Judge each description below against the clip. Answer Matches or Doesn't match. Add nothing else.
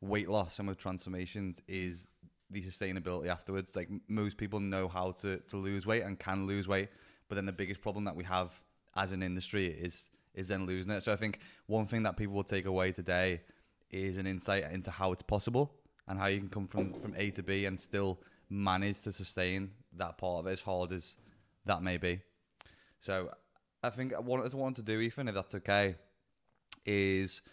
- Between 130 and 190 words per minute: Doesn't match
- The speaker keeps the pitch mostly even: Matches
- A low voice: Matches